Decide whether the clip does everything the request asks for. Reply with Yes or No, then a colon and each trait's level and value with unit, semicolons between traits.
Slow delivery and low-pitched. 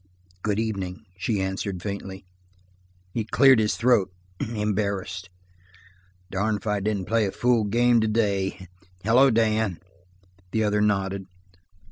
Yes: slow, 120 wpm; low, 105 Hz